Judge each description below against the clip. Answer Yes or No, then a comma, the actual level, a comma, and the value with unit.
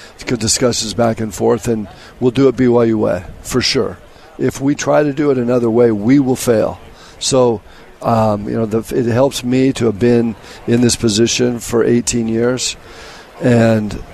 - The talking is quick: No, average, 185 wpm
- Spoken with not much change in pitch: Yes, narrow, 2.1 semitones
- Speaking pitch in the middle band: No, low, 120 Hz